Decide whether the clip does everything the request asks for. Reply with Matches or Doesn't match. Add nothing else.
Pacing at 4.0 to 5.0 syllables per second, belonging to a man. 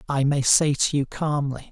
Matches